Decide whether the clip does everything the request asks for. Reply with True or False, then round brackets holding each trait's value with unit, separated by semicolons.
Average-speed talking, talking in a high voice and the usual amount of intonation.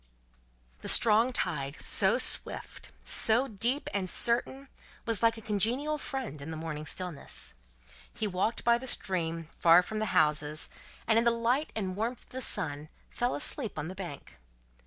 False (165 wpm; 215 Hz; 6.3 semitones)